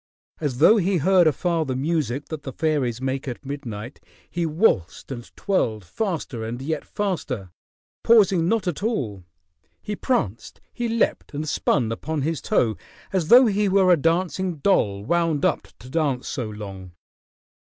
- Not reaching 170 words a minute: Yes, average, 160 wpm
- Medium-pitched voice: Yes, medium, 155 Hz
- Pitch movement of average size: No, wide, 7.2 semitones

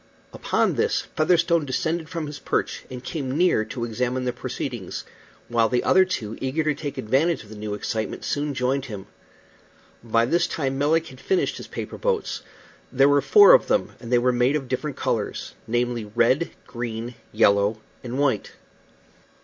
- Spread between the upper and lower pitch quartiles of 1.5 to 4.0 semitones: No, average, 4.5 semitones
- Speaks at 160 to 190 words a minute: Yes, average, 175 wpm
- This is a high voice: No, low, 130 Hz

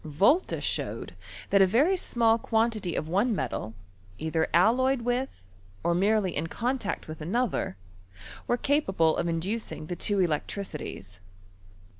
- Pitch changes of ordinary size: No, wide, 6.5 semitones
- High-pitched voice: Yes, high, 200 Hz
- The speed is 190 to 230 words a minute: No, slow, 135 wpm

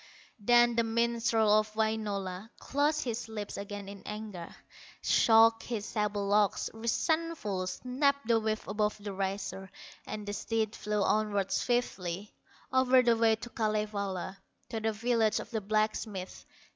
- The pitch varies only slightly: Yes, narrow, 2.3 semitones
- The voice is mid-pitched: No, high, 215 Hz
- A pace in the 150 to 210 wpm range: No, average, 140 wpm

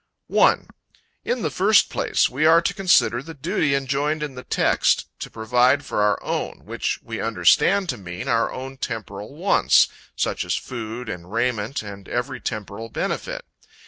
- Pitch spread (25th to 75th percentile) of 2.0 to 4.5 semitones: No, average, 5.2 semitones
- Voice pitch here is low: Yes, low, 125 Hz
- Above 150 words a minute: Yes, average, 165 wpm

